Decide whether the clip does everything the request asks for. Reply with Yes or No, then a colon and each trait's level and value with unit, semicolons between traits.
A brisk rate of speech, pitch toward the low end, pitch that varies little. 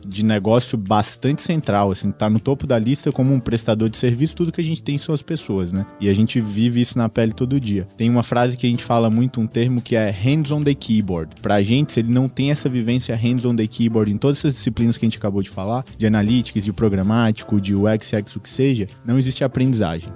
No: fast, 250 wpm; low, 115 Hz; average, 3.3 semitones